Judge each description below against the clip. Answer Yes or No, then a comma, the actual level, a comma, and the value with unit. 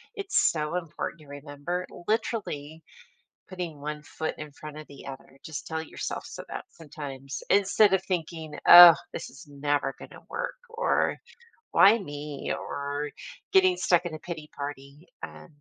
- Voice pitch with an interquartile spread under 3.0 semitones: No, average, 3.7 semitones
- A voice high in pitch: No, medium, 155 Hz